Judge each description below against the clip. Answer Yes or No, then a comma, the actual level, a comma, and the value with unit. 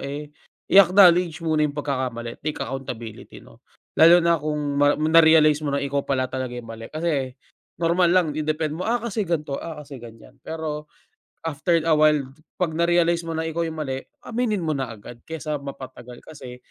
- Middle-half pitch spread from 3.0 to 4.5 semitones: Yes, average, 3.5 semitones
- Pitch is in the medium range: Yes, medium, 155 Hz